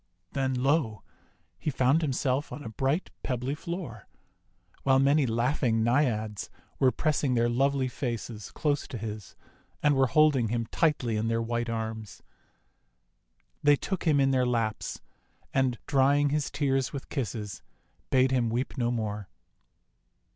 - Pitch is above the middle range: No, low, 130 Hz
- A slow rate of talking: No, average, 145 wpm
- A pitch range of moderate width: Yes, average, 3.6 semitones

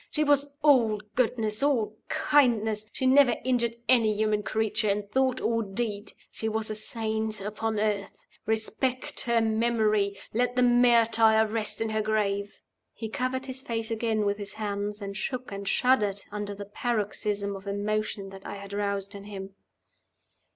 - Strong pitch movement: No, narrow, 2.5 semitones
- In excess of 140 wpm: Yes, average, 160 wpm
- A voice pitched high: Yes, high, 220 Hz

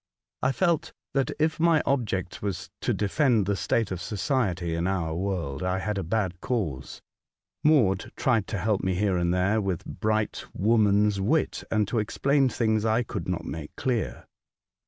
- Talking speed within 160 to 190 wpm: Yes, average, 170 wpm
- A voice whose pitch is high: No, low, 105 Hz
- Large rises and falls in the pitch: No, average, 4.3 semitones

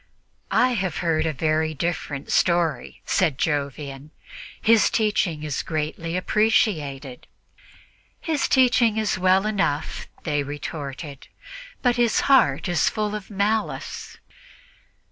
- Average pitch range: No, wide, 6.3 semitones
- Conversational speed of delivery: No, slow, 110 wpm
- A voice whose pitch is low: No, medium, 170 Hz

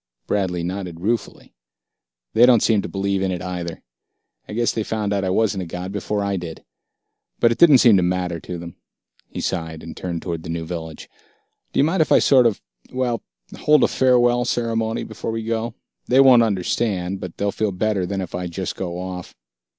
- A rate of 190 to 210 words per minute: Yes, fast, 205 wpm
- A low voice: Yes, low, 100 Hz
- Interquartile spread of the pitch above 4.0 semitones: Yes, average, 4.4 semitones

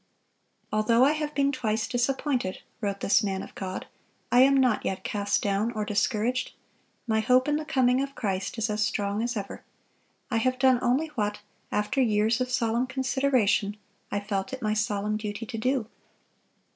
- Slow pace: No, average, 175 wpm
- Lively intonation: No, average, 3.7 semitones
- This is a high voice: Yes, high, 225 Hz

